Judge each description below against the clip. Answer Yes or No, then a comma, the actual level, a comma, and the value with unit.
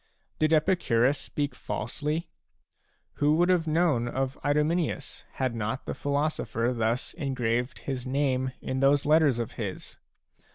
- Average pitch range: Yes, average, 3.8 semitones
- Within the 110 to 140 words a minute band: Yes, slow, 135 wpm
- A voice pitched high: No, medium, 140 Hz